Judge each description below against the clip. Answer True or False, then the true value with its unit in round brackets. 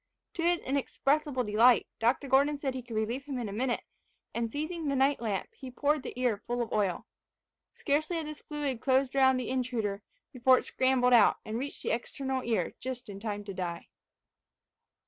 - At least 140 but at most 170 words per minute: False (190 wpm)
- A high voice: True (255 Hz)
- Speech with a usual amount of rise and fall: True (3.6 semitones)